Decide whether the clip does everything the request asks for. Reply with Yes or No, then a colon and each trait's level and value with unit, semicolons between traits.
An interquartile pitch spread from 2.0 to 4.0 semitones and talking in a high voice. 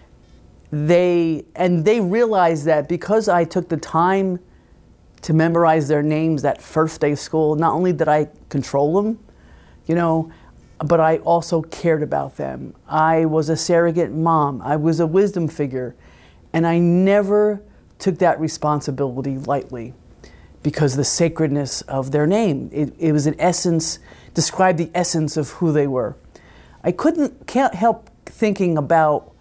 No: average, 2.9 semitones; medium, 160 Hz